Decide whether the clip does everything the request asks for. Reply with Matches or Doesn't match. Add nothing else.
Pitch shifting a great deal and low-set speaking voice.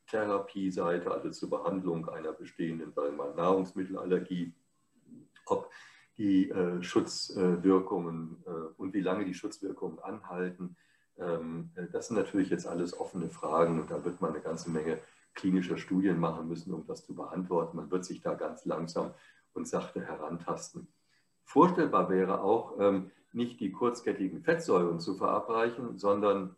Doesn't match